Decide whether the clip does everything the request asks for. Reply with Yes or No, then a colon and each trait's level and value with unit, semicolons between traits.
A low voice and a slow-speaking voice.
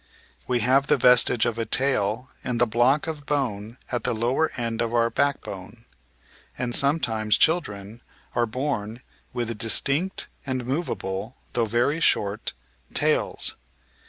No: low, 120 Hz; average, 145 wpm